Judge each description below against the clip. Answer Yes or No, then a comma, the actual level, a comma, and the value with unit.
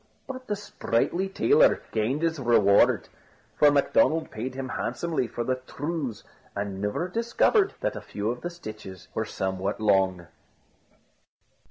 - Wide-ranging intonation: Yes, wide, 8.6 semitones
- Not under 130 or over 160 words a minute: Yes, average, 140 wpm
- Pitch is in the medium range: No, low, 130 Hz